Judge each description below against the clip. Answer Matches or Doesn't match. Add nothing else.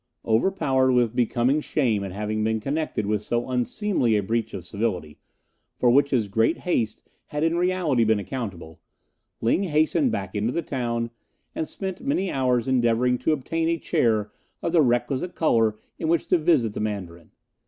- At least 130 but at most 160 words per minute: Doesn't match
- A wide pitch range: Matches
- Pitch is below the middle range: Matches